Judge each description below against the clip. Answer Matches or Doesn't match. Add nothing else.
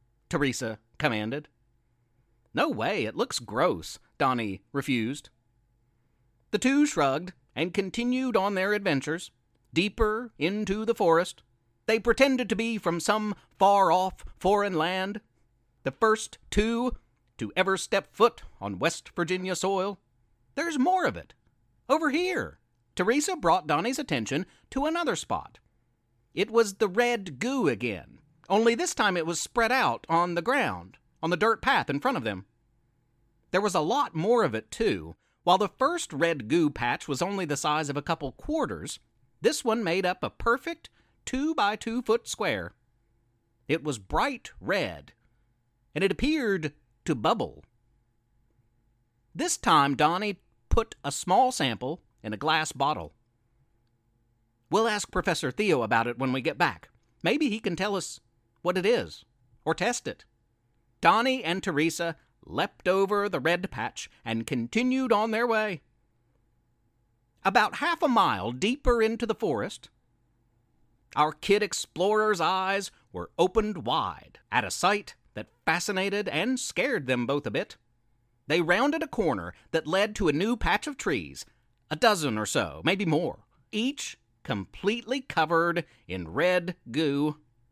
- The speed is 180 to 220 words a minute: Doesn't match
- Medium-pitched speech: Matches